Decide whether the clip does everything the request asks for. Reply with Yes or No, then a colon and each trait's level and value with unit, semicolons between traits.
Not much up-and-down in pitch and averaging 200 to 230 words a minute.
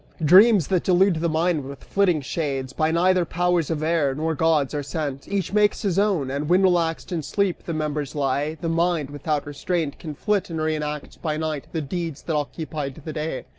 No: average, 3.2 semitones; fast, 205 wpm